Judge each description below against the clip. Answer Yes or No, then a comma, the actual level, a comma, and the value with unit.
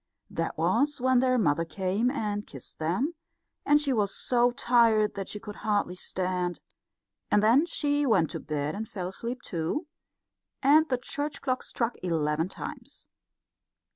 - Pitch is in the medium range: No, high, 220 Hz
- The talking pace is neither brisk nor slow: Yes, average, 155 wpm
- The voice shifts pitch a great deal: Yes, wide, 6.1 semitones